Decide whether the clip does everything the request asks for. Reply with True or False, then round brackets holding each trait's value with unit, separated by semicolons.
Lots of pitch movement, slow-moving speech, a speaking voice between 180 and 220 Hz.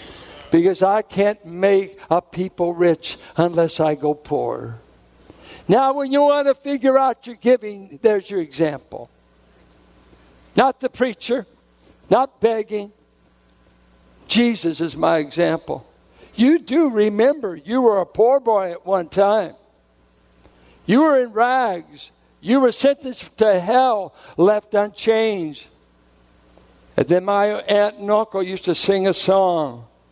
True (7.7 semitones; 130 wpm; 190 Hz)